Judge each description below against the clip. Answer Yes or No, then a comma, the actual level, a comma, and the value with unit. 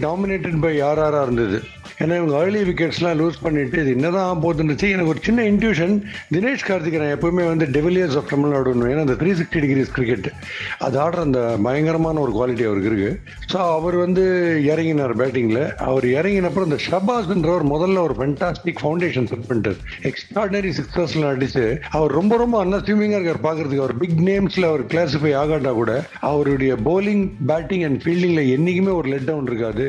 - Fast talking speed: Yes, fast, 165 wpm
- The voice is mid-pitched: Yes, medium, 160 Hz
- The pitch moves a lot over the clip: No, average, 4.5 semitones